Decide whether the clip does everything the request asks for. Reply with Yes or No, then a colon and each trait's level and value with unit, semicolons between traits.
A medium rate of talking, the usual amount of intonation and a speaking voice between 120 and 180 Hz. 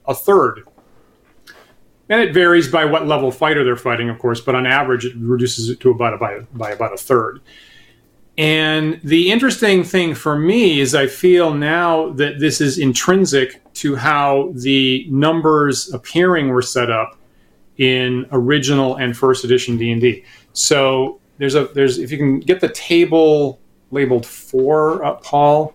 Yes: average, 170 wpm; average, 3.7 semitones; medium, 140 Hz